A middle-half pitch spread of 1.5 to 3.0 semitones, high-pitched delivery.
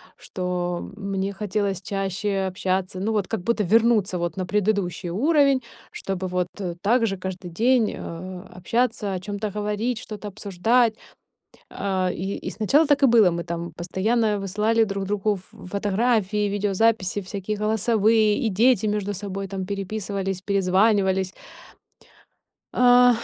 Yes: average, 2.7 semitones; high, 200 Hz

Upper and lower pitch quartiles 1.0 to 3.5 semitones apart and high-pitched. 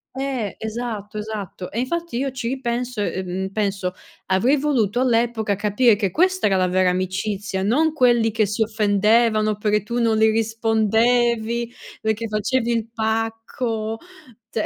Yes: narrow, 2.4 semitones; high, 220 Hz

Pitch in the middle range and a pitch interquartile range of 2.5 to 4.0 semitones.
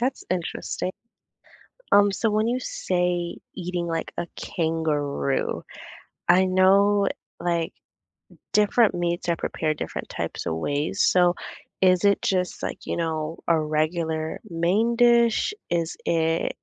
Yes: medium, 175 Hz; average, 3.6 semitones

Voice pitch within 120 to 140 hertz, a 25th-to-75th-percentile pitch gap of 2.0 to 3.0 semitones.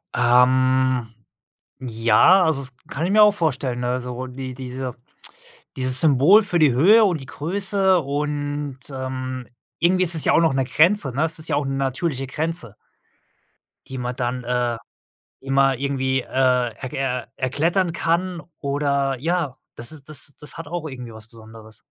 No: low, 135 Hz; average, 4.1 semitones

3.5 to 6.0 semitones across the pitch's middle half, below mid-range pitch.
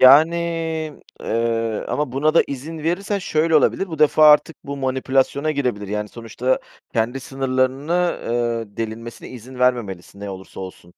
Yes: average, 4.7 semitones; low, 130 Hz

